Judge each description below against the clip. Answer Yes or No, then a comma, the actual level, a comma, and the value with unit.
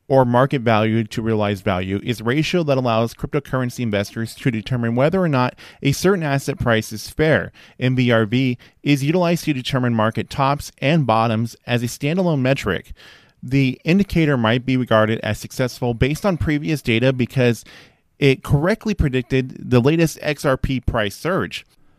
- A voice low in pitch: Yes, low, 130 Hz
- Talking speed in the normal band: Yes, average, 155 wpm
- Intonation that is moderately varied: Yes, average, 4.1 semitones